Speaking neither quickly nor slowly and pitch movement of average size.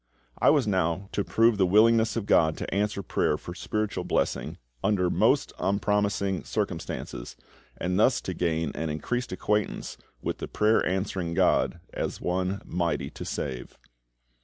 Yes: average, 150 wpm; average, 3.5 semitones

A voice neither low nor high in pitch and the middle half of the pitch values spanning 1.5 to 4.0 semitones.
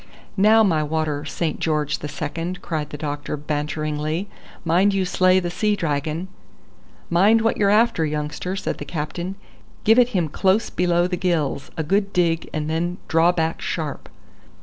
Yes: medium, 165 Hz; average, 3.6 semitones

